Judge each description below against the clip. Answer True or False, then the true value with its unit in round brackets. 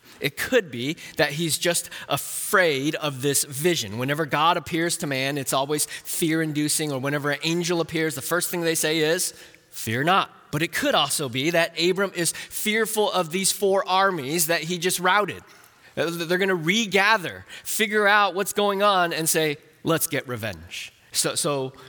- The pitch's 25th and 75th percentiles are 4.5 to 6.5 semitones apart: False (3.8 semitones)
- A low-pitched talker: False (165 Hz)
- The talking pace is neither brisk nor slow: True (180 wpm)